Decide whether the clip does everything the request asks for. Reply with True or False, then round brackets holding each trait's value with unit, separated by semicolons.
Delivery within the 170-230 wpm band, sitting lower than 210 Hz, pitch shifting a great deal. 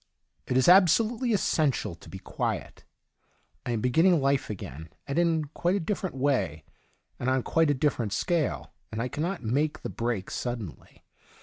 True (180 wpm; 140 Hz; 6.5 semitones)